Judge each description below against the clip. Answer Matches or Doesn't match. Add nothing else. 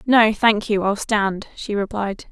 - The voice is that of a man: Doesn't match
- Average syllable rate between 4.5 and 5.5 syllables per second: Doesn't match